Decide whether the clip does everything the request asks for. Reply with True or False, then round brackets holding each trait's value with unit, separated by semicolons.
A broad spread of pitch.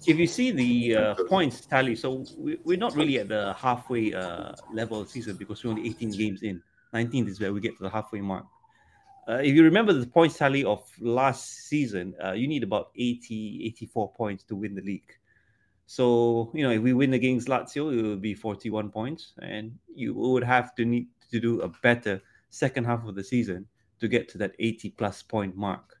False (3.3 semitones)